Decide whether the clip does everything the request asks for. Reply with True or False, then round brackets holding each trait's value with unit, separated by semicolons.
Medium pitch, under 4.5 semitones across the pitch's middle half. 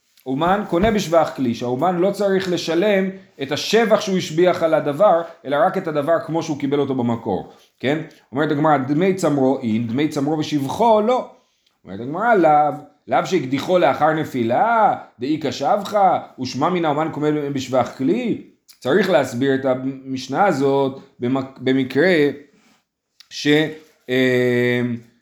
True (150 Hz; 4.1 semitones)